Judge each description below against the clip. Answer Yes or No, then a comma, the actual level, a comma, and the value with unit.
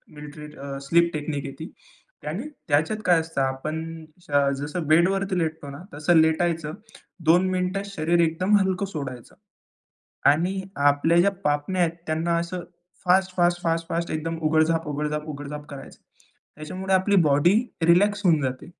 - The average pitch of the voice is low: No, medium, 165 Hz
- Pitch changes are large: No, average, 3.1 semitones